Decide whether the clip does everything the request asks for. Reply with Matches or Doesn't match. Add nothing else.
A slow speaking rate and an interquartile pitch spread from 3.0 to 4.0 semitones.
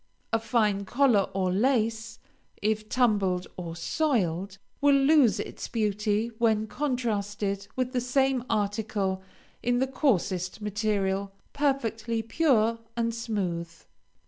Matches